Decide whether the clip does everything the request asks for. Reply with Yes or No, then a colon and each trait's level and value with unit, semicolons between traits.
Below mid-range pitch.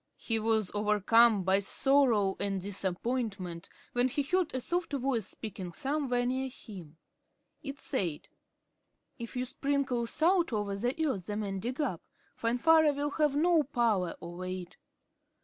No: high, 235 Hz